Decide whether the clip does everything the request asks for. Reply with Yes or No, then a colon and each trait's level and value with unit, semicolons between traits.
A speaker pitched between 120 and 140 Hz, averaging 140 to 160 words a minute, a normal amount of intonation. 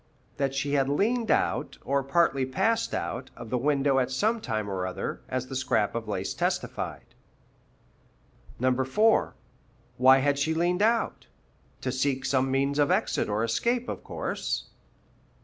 Yes: low, 135 Hz; average, 150 wpm; average, 3.8 semitones